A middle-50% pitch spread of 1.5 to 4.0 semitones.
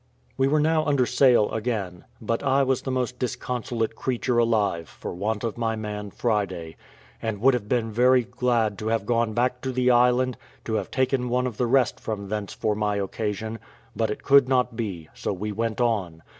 Yes: average, 3.0 semitones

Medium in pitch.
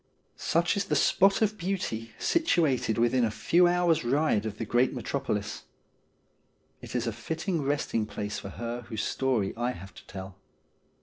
No: low, 125 Hz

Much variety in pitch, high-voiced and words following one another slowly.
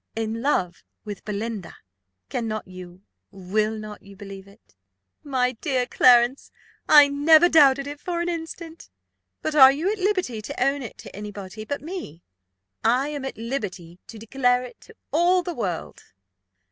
No: wide, 6.0 semitones; high, 245 Hz; average, 160 wpm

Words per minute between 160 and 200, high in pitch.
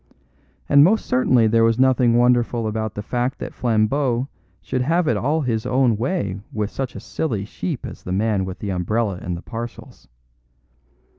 No: average, 175 wpm; low, 115 Hz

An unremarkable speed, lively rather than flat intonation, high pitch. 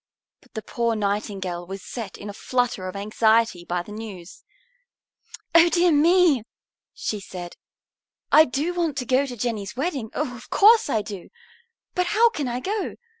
Yes: average, 170 wpm; wide, 7.3 semitones; high, 235 Hz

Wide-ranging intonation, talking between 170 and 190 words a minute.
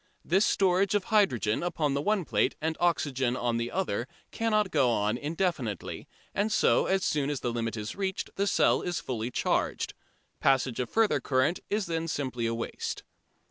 Yes: wide, 7.8 semitones; average, 175 wpm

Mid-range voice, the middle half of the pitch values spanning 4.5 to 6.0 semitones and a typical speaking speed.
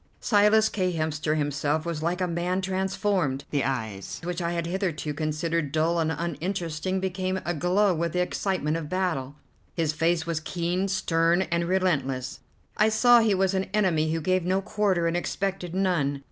No: medium, 170 Hz; average, 3.2 semitones; average, 170 wpm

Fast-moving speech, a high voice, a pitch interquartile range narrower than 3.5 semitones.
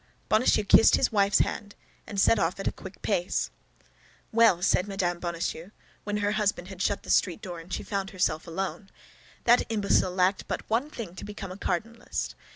No: average, 185 wpm; high, 195 Hz; average, 2.7 semitones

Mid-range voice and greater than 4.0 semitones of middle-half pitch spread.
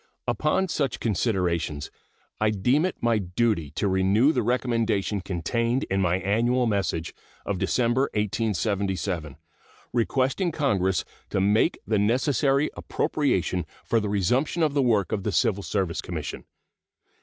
No: low, 110 Hz; average, 4.6 semitones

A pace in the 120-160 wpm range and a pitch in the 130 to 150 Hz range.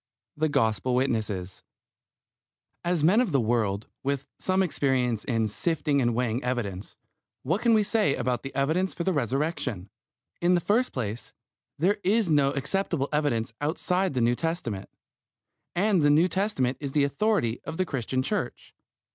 Yes: average, 155 wpm; medium, 140 Hz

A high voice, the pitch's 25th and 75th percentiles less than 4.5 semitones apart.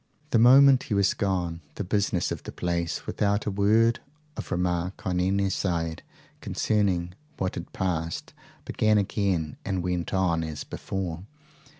No: very low, 95 Hz; average, 2.9 semitones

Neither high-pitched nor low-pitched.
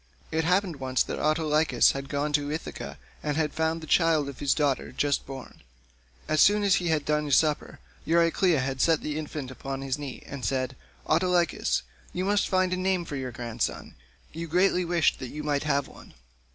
Yes: medium, 150 Hz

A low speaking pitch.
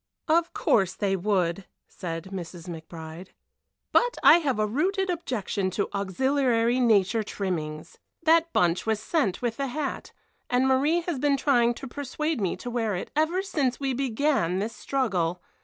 No: high, 235 Hz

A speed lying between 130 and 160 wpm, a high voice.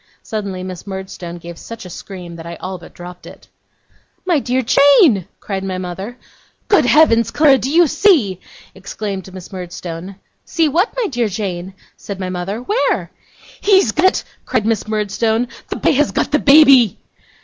No: average, 170 wpm; high, 210 Hz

